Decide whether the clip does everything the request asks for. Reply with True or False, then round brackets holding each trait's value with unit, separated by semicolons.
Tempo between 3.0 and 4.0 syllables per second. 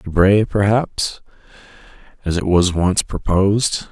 True (3.9 syllables/s)